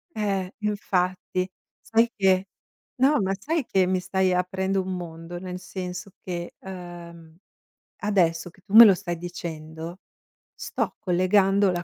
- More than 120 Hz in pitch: Yes, medium, 185 Hz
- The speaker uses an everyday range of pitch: No, narrow, 2.0 semitones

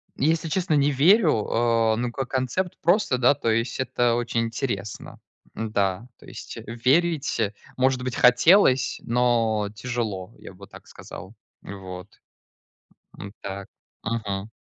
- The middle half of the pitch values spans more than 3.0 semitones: Yes, average, 3.5 semitones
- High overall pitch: No, low, 120 Hz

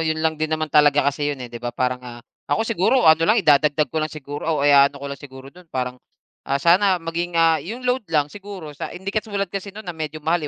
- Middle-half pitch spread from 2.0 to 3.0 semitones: No, average, 4.1 semitones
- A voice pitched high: No, medium, 155 Hz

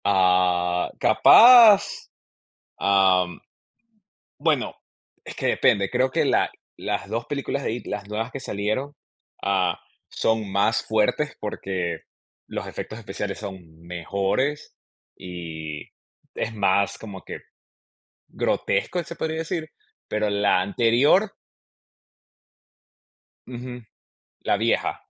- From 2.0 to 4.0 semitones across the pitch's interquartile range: No, average, 5.0 semitones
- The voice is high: No, low, 105 Hz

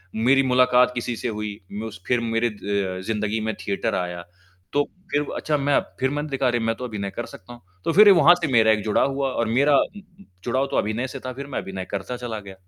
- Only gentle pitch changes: No, average, 3.9 semitones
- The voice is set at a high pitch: No, low, 120 Hz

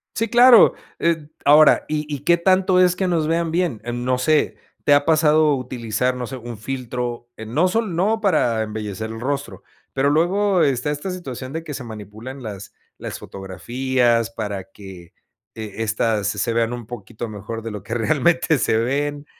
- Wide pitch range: Yes, wide, 6.0 semitones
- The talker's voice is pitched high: No, low, 130 Hz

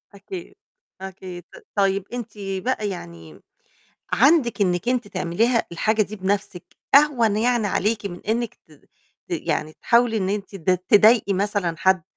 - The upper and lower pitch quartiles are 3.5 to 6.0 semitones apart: Yes, average, 3.8 semitones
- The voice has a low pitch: No, high, 205 Hz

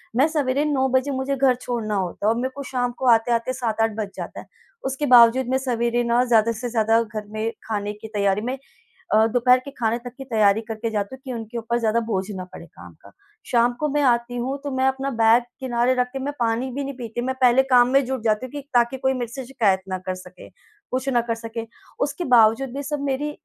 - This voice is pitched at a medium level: No, high, 240 Hz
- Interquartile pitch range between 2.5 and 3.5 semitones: Yes, average, 2.8 semitones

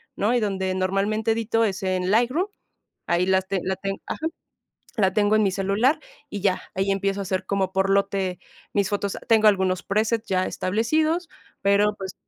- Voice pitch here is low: No, high, 195 Hz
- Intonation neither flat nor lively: No, narrow, 2.3 semitones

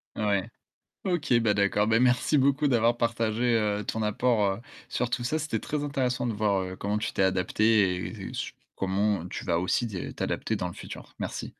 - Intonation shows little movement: No, average, 3.5 semitones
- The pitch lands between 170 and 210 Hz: No, low, 110 Hz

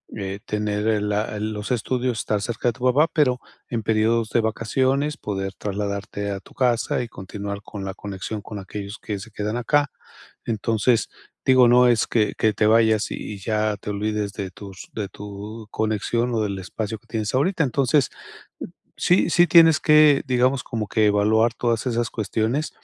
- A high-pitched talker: No, low, 110 Hz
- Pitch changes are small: No, average, 3.0 semitones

